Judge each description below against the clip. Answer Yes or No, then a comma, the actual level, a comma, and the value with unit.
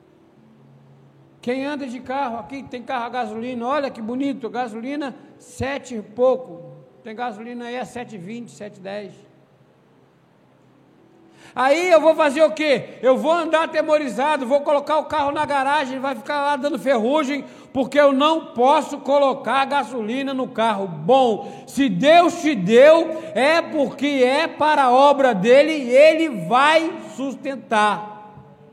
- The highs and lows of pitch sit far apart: No, average, 3.4 semitones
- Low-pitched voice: No, very high, 270 Hz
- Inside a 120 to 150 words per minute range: Yes, average, 140 wpm